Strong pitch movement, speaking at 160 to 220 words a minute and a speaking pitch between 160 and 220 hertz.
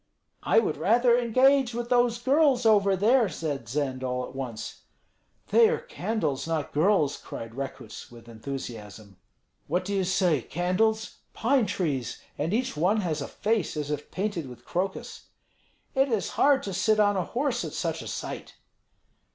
Yes: wide, 8.6 semitones; average, 165 wpm; high, 190 Hz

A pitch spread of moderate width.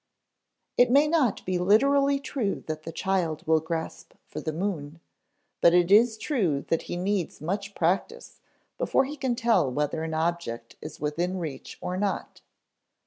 No: wide, 6.2 semitones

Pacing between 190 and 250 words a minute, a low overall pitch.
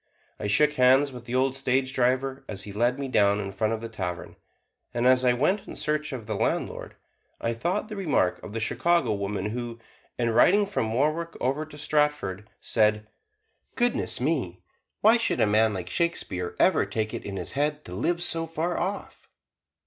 Yes: average, 195 wpm; low, 125 Hz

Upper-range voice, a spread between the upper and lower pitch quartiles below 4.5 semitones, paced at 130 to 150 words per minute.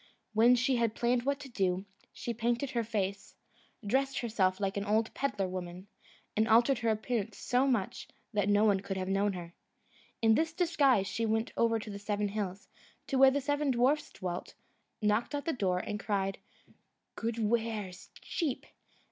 No: high, 220 Hz; average, 3.8 semitones; average, 175 wpm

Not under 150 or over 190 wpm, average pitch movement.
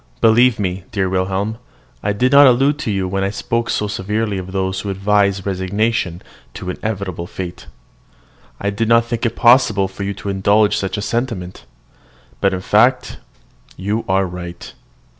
Yes: average, 165 wpm; average, 3.0 semitones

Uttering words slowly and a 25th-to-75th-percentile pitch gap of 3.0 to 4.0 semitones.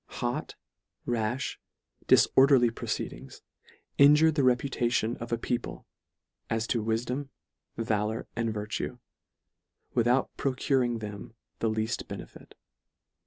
No: slow, 105 wpm; narrow, 2.5 semitones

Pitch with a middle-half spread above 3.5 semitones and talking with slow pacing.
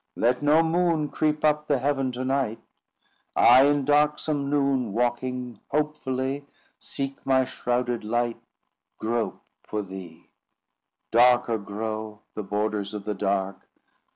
Yes: average, 4.7 semitones; slow, 125 wpm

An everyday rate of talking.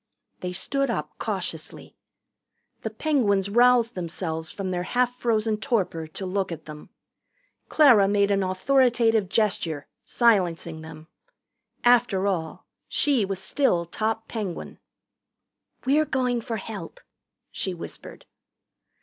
No: slow, 115 wpm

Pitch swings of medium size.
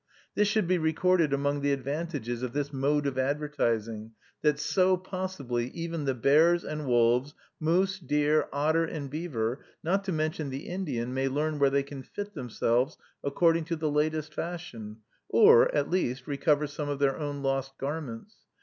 Yes: average, 3.6 semitones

